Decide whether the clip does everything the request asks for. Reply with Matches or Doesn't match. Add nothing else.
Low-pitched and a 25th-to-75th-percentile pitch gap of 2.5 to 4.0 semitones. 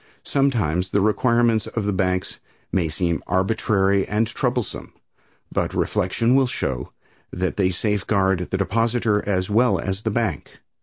Matches